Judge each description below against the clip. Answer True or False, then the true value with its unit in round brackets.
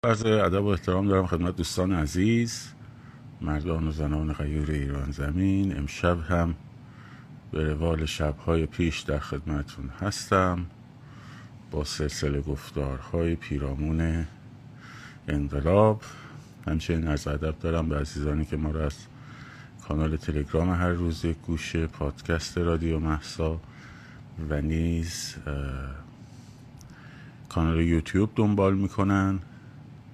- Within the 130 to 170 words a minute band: False (105 wpm)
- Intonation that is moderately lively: False (6.2 semitones)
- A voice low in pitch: True (85 Hz)